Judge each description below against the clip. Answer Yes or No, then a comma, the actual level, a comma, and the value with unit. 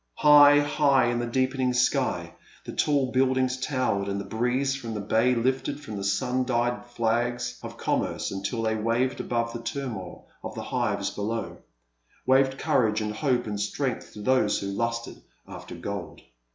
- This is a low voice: Yes, low, 120 Hz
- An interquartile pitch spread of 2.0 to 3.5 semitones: Yes, average, 2.9 semitones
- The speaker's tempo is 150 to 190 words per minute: Yes, average, 170 wpm